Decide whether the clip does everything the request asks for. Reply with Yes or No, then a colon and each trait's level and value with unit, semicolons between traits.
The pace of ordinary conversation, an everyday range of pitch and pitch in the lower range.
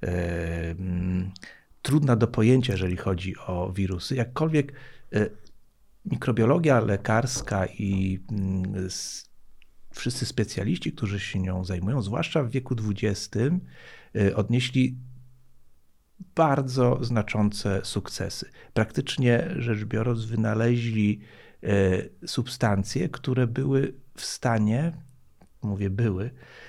No: slow, 80 wpm; average, 4.8 semitones; low, 115 Hz